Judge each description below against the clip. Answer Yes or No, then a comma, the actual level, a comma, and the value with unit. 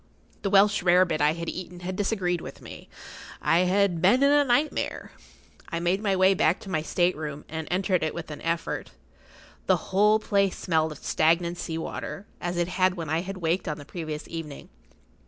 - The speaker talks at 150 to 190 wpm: No, average, 200 wpm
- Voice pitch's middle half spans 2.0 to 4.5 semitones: Yes, average, 3.1 semitones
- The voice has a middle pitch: Yes, medium, 175 Hz